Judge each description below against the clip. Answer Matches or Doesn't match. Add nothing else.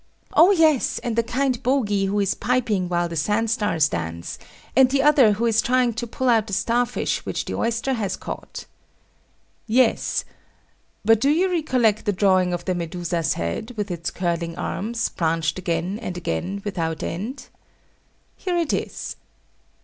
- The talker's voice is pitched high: Matches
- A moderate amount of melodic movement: Doesn't match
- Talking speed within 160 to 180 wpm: Matches